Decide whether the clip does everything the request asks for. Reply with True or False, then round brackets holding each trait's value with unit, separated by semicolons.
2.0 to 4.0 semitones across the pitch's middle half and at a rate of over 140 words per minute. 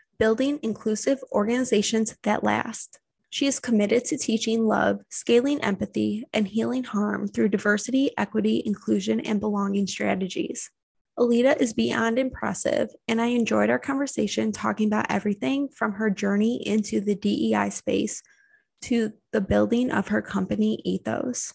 False (3.4 semitones; 135 wpm)